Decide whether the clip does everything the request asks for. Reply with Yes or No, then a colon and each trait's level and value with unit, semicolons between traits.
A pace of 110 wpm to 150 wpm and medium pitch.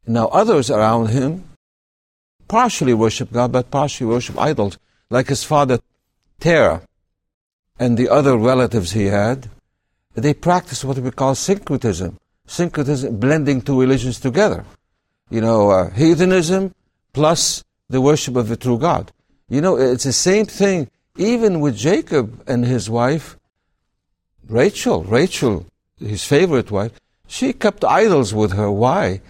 No: slow, 135 wpm; low, 125 Hz